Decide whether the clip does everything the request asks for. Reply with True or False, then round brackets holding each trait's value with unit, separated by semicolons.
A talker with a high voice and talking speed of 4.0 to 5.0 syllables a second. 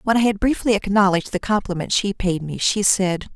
False (200 Hz; 5.7 syllables/s)